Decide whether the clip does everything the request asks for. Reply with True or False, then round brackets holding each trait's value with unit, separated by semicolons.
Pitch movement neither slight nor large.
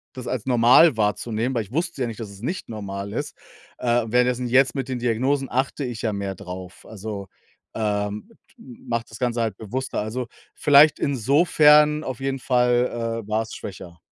True (3.6 semitones)